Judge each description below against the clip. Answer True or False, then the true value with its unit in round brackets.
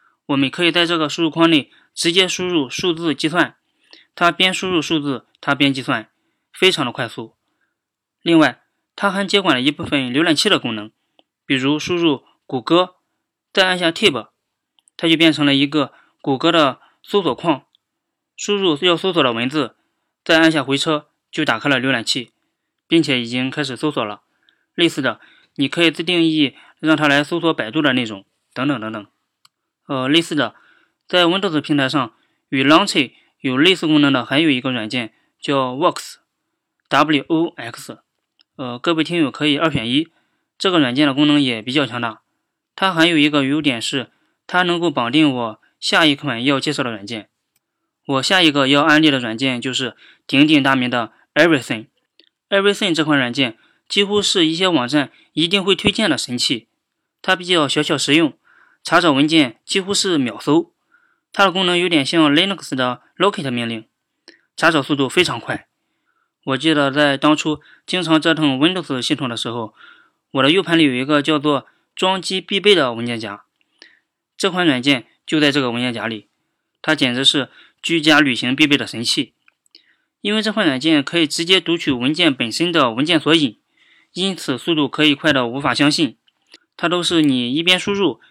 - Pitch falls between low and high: True (155 Hz)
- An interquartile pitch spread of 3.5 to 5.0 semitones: True (4.7 semitones)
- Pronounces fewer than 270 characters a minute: False (285 characters per minute)